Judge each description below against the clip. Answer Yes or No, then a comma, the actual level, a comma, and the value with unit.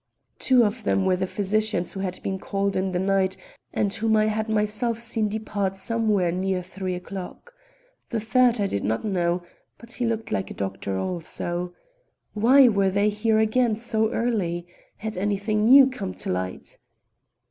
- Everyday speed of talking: Yes, average, 170 wpm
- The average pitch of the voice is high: Yes, high, 205 Hz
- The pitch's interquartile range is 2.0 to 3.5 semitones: Yes, average, 3.0 semitones